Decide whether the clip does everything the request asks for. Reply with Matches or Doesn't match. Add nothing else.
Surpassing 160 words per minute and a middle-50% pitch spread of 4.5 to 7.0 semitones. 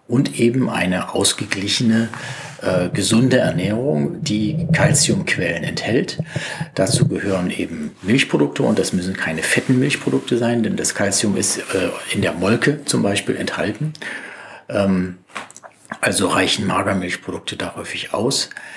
Doesn't match